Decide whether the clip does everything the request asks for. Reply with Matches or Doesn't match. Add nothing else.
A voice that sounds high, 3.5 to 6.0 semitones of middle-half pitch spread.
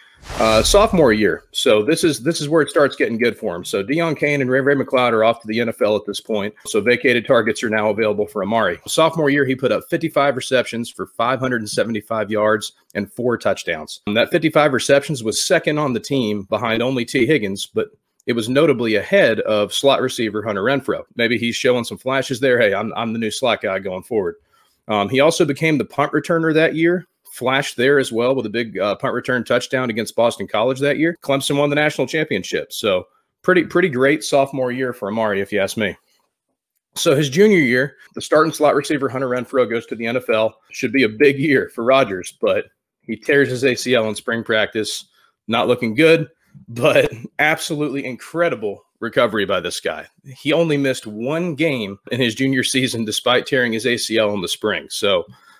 Doesn't match